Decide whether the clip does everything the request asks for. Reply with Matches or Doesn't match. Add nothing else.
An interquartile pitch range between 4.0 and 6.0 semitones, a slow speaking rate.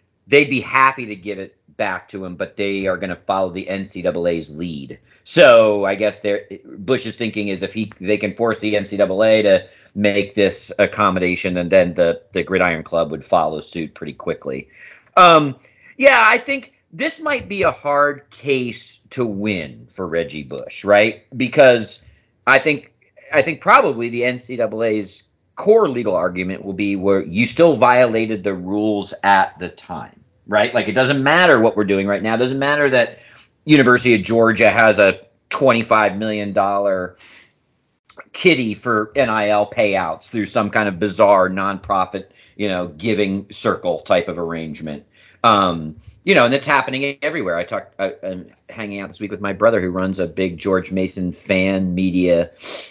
Doesn't match